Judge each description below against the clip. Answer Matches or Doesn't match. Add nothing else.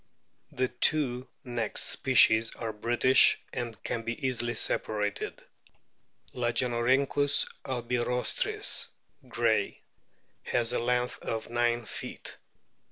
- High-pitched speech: Doesn't match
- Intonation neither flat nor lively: Doesn't match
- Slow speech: Matches